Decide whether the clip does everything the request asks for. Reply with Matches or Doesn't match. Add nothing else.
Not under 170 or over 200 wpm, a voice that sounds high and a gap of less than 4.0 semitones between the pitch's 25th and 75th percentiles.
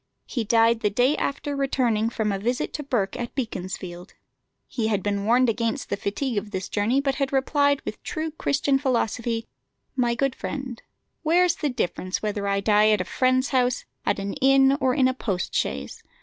Doesn't match